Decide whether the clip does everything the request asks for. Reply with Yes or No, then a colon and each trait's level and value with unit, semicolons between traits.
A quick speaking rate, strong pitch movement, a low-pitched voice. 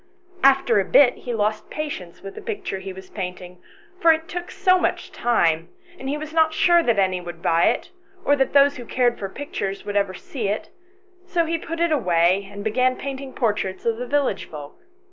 No: fast, 210 wpm; wide, 8.1 semitones; high, 240 Hz